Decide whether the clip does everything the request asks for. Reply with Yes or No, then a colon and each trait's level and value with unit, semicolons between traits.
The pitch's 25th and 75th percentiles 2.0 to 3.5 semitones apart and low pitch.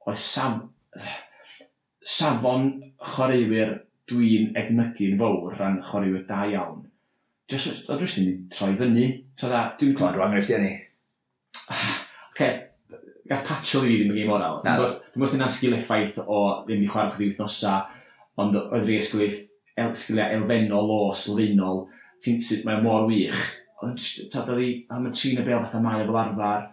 Yes: average, 3.0 semitones; low, 110 Hz